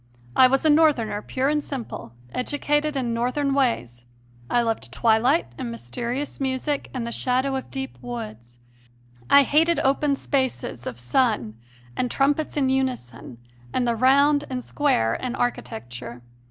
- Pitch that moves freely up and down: No, average, 4.1 semitones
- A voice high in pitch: Yes, very high, 255 Hz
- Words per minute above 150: No, average, 145 wpm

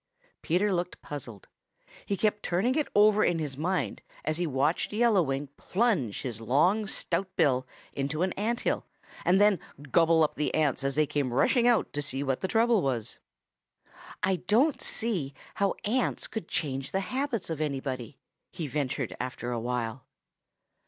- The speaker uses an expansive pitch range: Yes, wide, 7.1 semitones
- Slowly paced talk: No, average, 165 wpm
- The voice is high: No, medium, 160 Hz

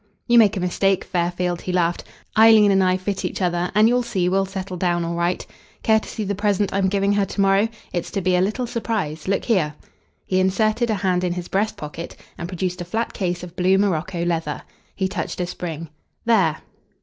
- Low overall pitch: No, medium, 185 Hz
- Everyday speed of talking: No, fast, 215 wpm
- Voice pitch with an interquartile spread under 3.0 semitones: Yes, narrow, 2.5 semitones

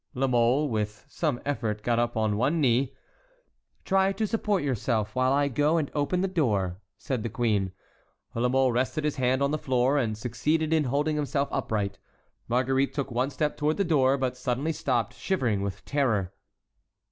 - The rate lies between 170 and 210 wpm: Yes, average, 180 wpm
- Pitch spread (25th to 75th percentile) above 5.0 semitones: No, average, 4.0 semitones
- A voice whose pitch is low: Yes, low, 130 Hz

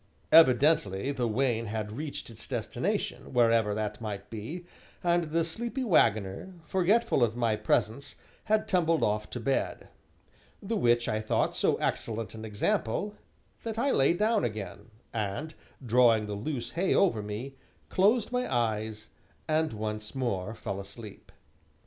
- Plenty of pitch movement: Yes, wide, 7.3 semitones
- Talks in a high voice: No, low, 120 Hz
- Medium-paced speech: Yes, average, 145 wpm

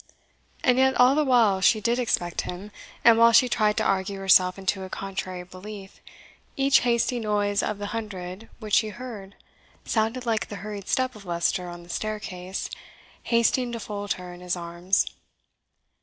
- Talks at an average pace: Yes, average, 170 wpm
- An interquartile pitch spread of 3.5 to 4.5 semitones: Yes, average, 3.8 semitones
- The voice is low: No, high, 205 Hz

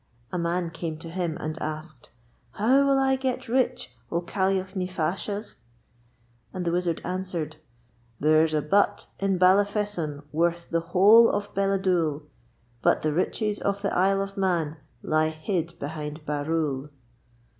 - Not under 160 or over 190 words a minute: No, average, 145 wpm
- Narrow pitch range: No, average, 4.0 semitones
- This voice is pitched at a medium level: Yes, medium, 175 Hz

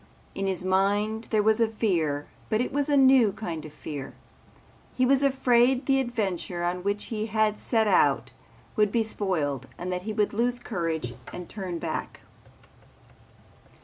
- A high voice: Yes, high, 210 Hz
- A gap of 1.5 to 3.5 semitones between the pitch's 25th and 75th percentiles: No, average, 4.7 semitones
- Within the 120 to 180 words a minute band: Yes, average, 160 wpm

